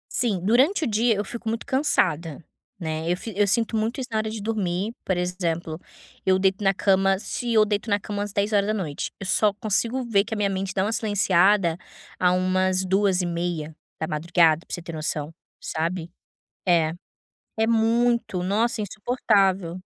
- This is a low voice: No, high, 195 Hz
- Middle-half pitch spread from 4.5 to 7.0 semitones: No, average, 3.6 semitones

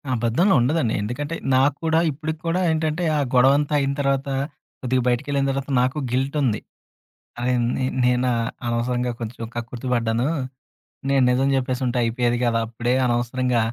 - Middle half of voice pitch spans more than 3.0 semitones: No, average, 2.7 semitones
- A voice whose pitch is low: Yes, low, 125 Hz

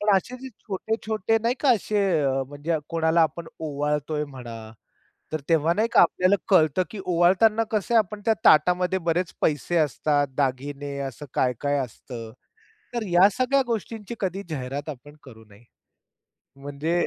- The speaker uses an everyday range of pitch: No, wide, 5.8 semitones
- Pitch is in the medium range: Yes, medium, 165 Hz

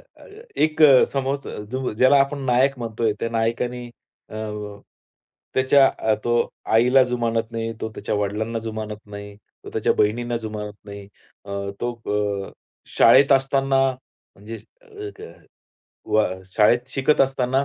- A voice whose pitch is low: Yes, low, 120 Hz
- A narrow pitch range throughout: No, average, 3.6 semitones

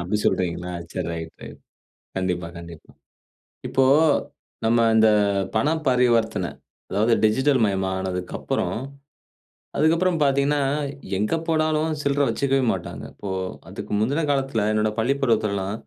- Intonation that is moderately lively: No, wide, 6.6 semitones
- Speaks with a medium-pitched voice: No, low, 110 Hz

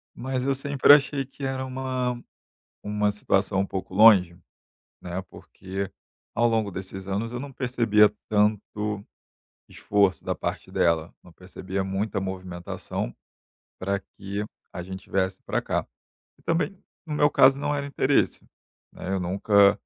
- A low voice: Yes, low, 105 Hz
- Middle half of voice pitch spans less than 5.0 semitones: No, average, 5.3 semitones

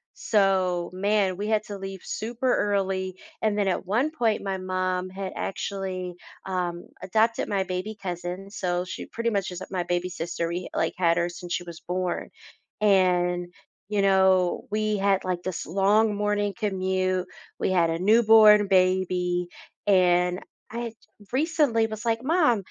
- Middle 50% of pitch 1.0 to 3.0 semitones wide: Yes, narrow, 2.6 semitones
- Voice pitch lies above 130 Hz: Yes, high, 190 Hz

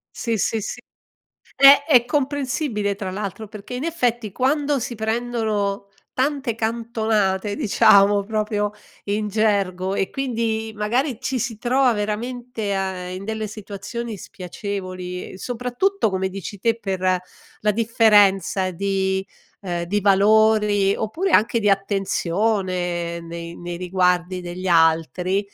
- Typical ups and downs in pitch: Yes, average, 3.4 semitones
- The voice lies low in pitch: No, high, 210 Hz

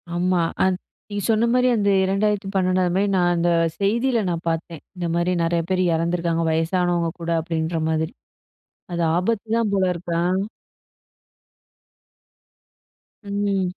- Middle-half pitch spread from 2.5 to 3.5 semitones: Yes, average, 3.0 semitones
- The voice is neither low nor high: Yes, medium, 180 Hz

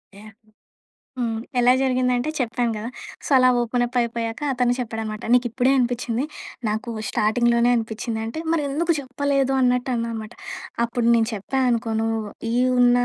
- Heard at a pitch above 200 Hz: Yes, high, 240 Hz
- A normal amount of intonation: No, narrow, 1.9 semitones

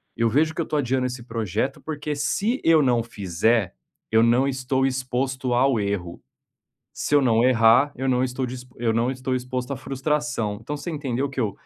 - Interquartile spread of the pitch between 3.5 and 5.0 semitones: No, average, 2.8 semitones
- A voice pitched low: Yes, low, 130 Hz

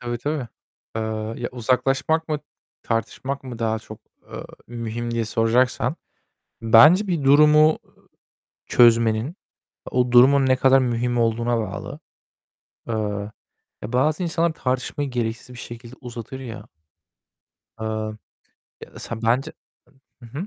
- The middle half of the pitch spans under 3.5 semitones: Yes, average, 3.0 semitones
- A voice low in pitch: Yes, low, 120 Hz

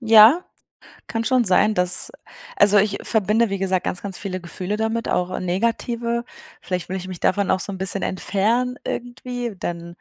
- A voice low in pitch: No, high, 200 Hz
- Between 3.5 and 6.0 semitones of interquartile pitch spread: Yes, average, 3.8 semitones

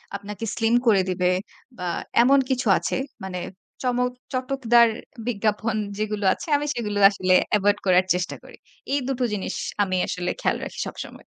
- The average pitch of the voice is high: Yes, high, 210 Hz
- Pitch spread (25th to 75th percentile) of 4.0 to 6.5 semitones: Yes, average, 4.4 semitones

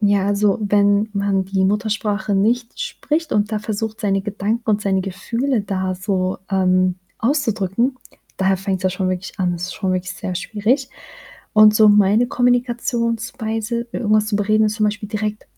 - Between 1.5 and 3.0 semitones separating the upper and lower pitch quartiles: Yes, narrow, 2.6 semitones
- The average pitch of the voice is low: No, high, 210 Hz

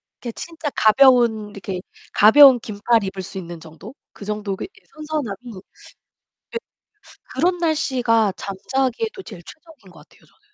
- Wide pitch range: Yes, wide, 6.2 semitones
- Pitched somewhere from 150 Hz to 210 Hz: No, high, 230 Hz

